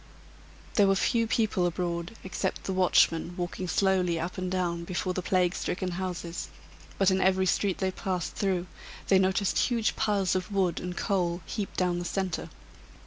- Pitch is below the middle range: No, medium, 185 Hz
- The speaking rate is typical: Yes, average, 170 wpm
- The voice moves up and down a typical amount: No, narrow, 1.6 semitones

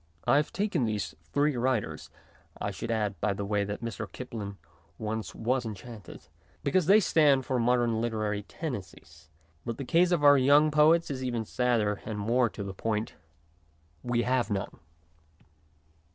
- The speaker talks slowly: No, average, 160 wpm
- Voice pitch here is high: No, low, 120 Hz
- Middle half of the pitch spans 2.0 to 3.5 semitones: No, average, 4.5 semitones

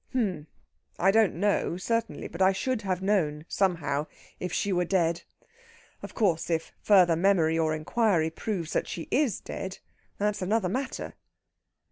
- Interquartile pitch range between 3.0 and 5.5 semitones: Yes, average, 3.9 semitones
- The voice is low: No, medium, 185 Hz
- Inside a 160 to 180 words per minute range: No, average, 150 wpm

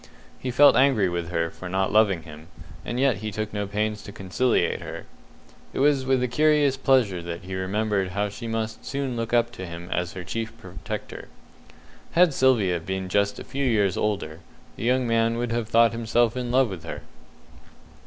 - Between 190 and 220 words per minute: Yes, average, 195 wpm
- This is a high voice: No, low, 110 Hz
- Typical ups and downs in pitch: Yes, average, 4.5 semitones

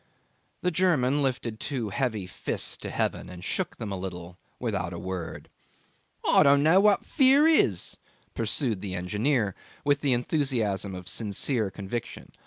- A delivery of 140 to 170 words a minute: Yes, average, 150 wpm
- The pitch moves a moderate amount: No, wide, 6.9 semitones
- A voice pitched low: Yes, low, 115 Hz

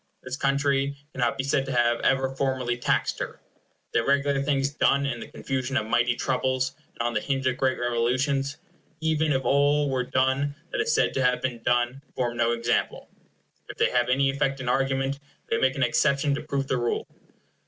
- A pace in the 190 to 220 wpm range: Yes, average, 195 wpm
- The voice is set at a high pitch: No, low, 135 Hz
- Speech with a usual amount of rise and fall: No, narrow, 2.1 semitones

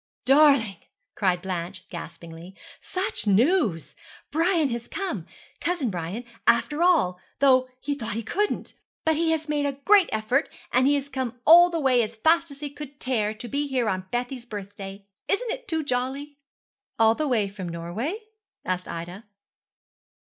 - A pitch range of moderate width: No, wide, 6.8 semitones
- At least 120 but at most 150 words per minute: No, average, 160 wpm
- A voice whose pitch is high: Yes, very high, 255 Hz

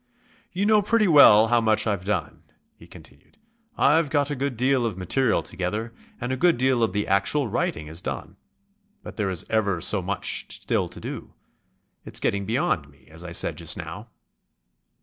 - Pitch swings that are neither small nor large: No, wide, 6.4 semitones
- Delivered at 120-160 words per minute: No, average, 185 wpm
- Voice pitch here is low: Yes, low, 110 Hz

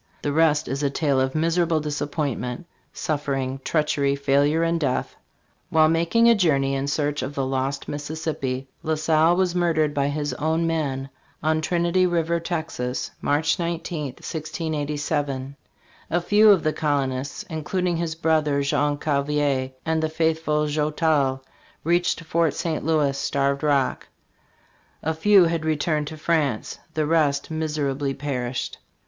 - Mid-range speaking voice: Yes, medium, 150 Hz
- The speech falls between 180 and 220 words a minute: No, average, 150 wpm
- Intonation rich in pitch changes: No, narrow, 2.6 semitones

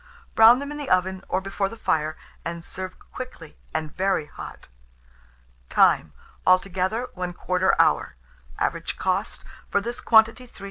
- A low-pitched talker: No, high, 190 Hz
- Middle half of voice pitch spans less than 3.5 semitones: No, average, 4.0 semitones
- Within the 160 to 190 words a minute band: No, average, 140 wpm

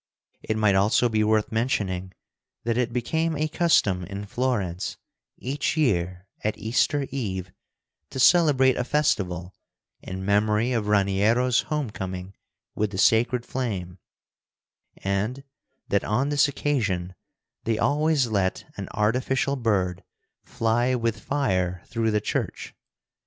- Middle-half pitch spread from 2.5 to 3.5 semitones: No, average, 5.1 semitones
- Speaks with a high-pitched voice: No, low, 110 Hz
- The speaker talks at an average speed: No, slow, 125 wpm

